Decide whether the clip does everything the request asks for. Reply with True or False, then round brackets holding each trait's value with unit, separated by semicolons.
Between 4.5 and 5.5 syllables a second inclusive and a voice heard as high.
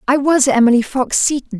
True (5.3 syllables/s; 260 Hz)